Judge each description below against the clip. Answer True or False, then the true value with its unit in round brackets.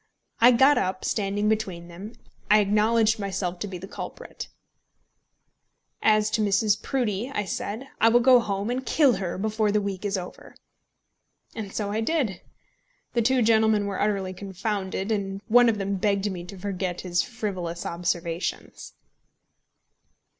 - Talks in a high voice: True (205 Hz)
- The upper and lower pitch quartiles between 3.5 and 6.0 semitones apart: False (2.6 semitones)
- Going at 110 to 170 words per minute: True (155 wpm)